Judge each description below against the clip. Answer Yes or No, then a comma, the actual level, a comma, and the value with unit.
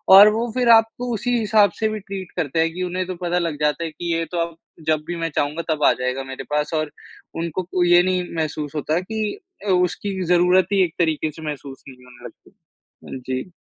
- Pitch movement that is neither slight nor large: Yes, average, 3.8 semitones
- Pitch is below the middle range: No, medium, 175 Hz